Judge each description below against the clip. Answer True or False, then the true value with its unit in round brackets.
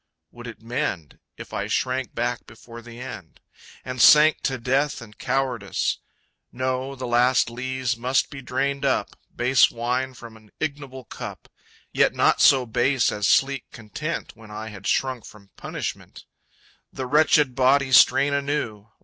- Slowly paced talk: False (150 wpm)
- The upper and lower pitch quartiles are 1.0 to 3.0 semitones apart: True (2.5 semitones)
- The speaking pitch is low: True (125 Hz)